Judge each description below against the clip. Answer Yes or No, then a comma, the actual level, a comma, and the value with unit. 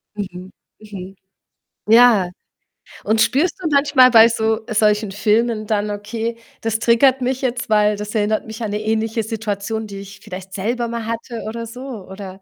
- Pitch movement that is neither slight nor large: No, narrow, 2.1 semitones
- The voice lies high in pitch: Yes, high, 220 Hz